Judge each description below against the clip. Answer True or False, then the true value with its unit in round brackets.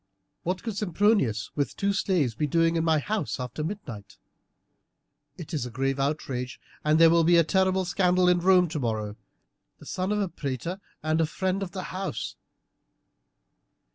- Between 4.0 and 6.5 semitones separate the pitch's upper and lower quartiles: True (5.0 semitones)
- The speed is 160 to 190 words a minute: True (170 wpm)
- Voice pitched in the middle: True (165 Hz)